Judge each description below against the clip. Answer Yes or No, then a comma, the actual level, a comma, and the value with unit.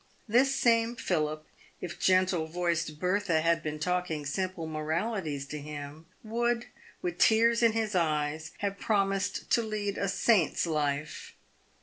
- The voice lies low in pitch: No, medium, 180 Hz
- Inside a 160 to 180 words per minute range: No, slow, 135 wpm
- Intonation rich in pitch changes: Yes, wide, 5.7 semitones